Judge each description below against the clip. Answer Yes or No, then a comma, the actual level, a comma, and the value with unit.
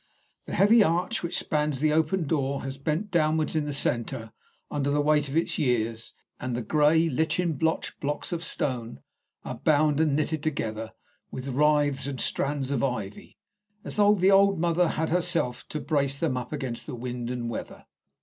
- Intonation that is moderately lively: Yes, average, 3.8 semitones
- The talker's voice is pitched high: No, medium, 150 Hz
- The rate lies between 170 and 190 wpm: Yes, average, 180 wpm